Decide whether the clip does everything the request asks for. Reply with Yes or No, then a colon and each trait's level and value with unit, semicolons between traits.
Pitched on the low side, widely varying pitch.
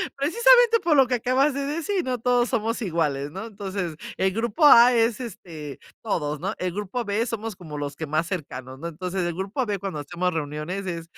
No: high, 195 Hz; wide, 6.8 semitones